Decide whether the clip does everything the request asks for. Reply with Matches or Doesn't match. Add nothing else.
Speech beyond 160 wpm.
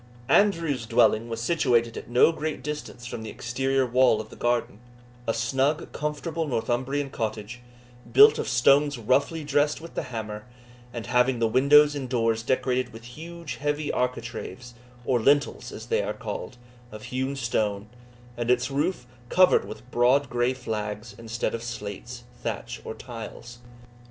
Doesn't match